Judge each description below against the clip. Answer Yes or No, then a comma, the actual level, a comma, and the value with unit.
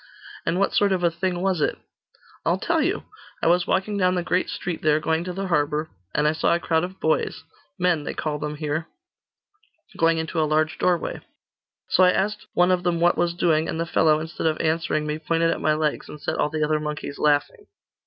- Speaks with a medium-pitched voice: Yes, medium, 165 Hz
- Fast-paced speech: Yes, fast, 225 wpm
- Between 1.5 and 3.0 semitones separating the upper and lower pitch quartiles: Yes, narrow, 2.6 semitones